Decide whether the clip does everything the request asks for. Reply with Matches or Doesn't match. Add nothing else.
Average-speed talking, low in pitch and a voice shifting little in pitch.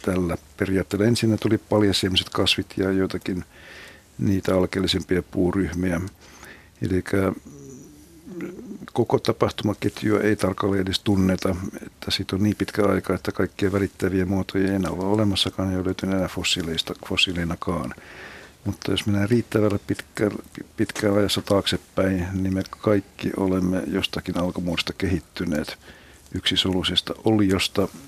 Matches